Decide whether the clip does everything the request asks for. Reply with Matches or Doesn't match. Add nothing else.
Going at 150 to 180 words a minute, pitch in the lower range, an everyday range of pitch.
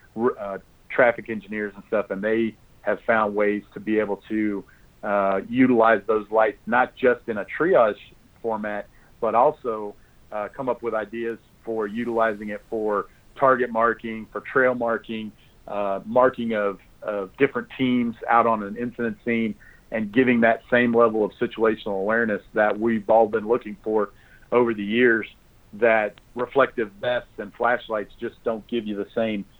Doesn't match